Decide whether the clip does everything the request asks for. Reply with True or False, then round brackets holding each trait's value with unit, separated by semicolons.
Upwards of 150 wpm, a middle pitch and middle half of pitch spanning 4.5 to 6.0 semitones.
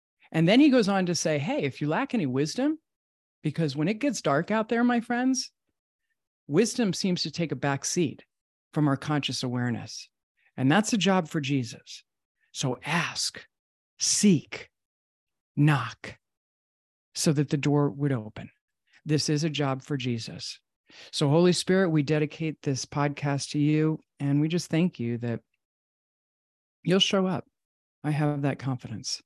True (160 wpm; 150 Hz; 4.8 semitones)